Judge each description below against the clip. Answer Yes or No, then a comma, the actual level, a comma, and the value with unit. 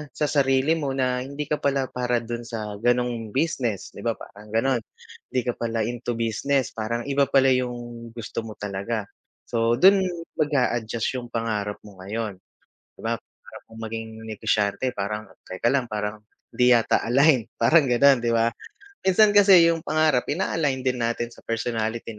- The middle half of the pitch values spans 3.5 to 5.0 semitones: No, average, 3.1 semitones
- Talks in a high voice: No, low, 120 Hz